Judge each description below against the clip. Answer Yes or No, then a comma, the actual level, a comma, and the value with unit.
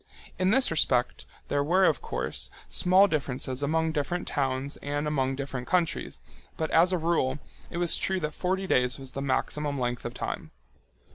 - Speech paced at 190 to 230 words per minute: No, average, 170 wpm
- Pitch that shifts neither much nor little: Yes, average, 4.6 semitones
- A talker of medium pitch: Yes, medium, 150 Hz